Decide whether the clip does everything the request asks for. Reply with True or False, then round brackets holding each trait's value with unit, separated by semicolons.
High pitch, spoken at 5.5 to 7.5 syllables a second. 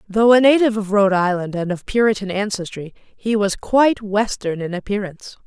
True (205 Hz; 5.6 syllables/s)